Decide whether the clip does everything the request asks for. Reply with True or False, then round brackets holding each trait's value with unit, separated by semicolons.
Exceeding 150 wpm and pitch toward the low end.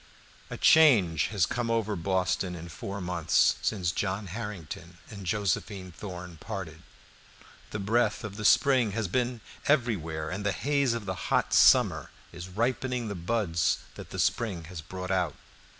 True (160 wpm; 100 Hz)